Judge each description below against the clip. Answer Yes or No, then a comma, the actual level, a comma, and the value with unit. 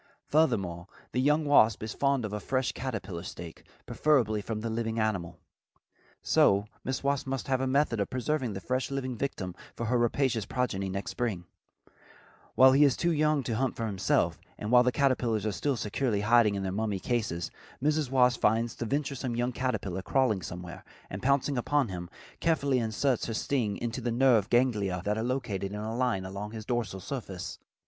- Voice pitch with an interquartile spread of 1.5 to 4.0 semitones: No, average, 4.4 semitones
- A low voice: Yes, low, 120 Hz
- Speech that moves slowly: No, average, 185 wpm